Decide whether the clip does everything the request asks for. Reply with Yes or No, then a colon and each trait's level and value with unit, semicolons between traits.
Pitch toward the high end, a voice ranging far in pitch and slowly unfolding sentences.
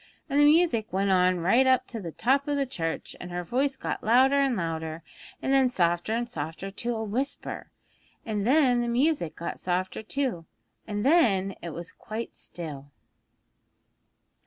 No: high, 220 Hz; wide, 7.0 semitones; average, 170 wpm